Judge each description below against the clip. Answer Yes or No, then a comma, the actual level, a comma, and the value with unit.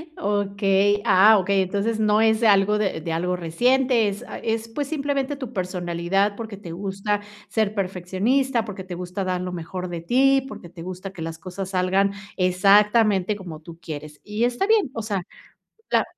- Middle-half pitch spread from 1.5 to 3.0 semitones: No, average, 3.4 semitones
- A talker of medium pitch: No, high, 200 Hz